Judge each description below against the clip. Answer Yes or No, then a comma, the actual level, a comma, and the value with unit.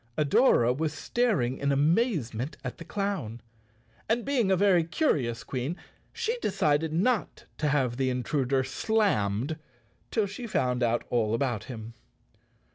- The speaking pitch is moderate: Yes, medium, 145 Hz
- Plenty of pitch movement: Yes, wide, 8.3 semitones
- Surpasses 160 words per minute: No, slow, 135 wpm